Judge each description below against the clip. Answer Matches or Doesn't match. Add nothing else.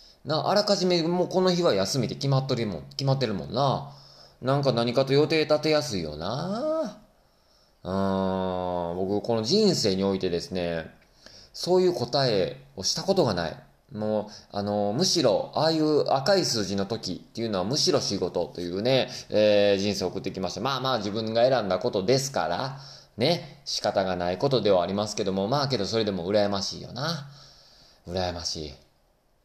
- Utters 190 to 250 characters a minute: Doesn't match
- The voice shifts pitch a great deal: Matches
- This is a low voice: Matches